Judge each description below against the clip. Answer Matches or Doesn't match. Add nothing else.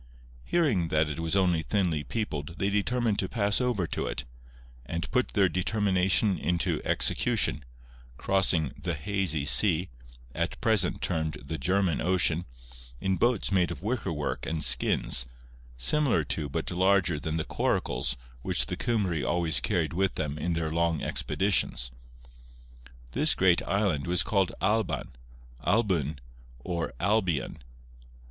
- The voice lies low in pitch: Matches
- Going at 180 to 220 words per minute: Doesn't match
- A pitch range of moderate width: Matches